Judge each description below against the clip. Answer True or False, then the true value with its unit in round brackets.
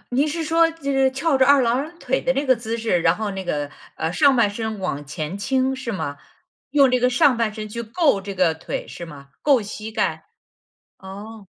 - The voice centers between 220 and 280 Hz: True (230 Hz)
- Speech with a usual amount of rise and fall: False (5.7 semitones)